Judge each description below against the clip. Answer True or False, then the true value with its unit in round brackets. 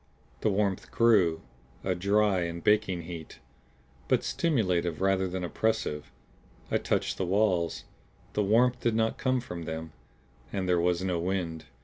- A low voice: True (95 Hz)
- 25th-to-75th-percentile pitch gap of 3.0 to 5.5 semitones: True (3.8 semitones)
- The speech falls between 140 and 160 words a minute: True (145 wpm)